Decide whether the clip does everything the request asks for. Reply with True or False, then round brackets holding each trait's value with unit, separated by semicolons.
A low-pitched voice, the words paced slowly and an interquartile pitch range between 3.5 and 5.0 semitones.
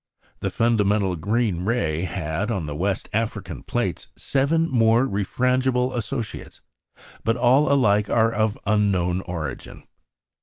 True (105 Hz; 120 wpm; 4.5 semitones)